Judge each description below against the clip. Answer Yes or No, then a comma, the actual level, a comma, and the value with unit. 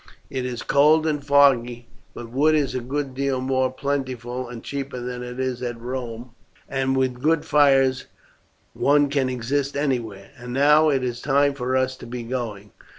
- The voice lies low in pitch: Yes, low, 130 Hz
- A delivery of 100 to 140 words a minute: No, average, 175 wpm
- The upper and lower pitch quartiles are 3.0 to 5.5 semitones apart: No, narrow, 2.4 semitones